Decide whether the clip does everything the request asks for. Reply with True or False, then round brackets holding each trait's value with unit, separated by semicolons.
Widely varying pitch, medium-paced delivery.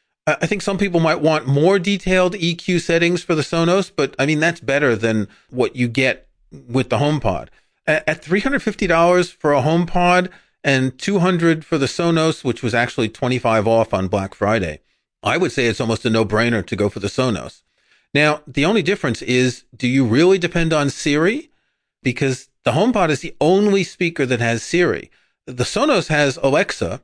True (6.1 semitones; 180 wpm)